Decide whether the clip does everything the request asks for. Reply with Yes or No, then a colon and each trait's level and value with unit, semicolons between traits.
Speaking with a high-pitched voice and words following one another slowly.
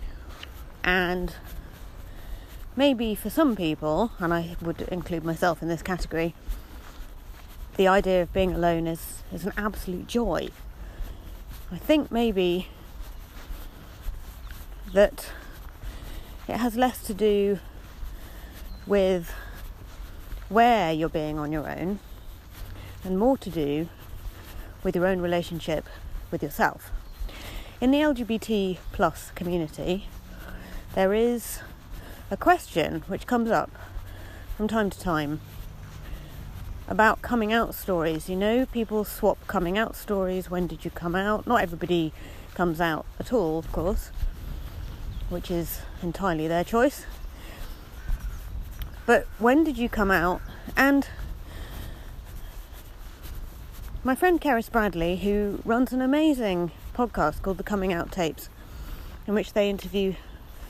No: medium, 165 Hz; slow, 120 wpm